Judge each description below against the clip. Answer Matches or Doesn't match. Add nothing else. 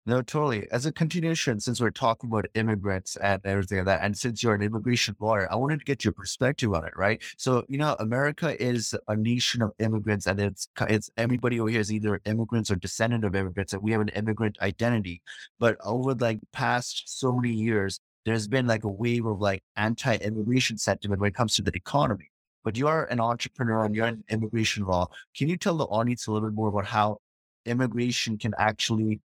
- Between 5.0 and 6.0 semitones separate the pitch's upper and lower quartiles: Doesn't match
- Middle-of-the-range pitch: Doesn't match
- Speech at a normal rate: Doesn't match